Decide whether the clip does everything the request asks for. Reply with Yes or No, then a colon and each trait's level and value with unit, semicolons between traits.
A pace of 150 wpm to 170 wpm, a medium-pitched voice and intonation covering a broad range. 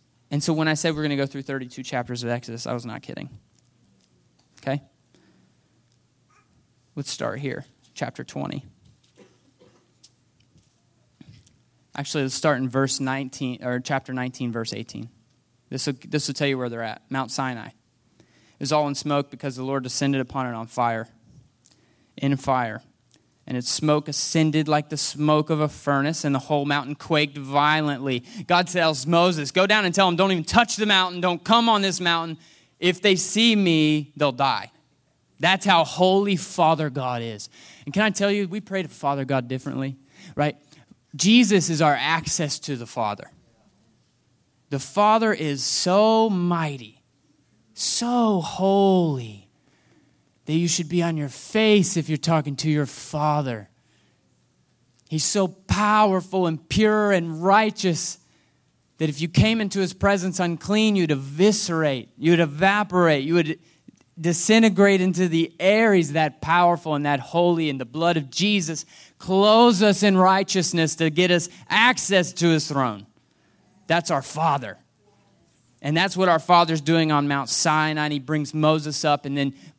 No: average, 155 wpm; medium, 155 Hz; average, 4.9 semitones